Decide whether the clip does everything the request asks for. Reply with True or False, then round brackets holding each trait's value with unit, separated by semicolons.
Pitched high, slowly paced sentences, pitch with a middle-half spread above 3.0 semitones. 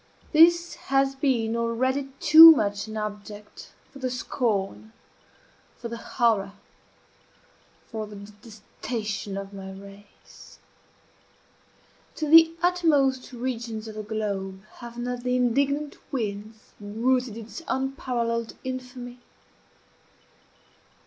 True (235 Hz; 105 wpm; 3.9 semitones)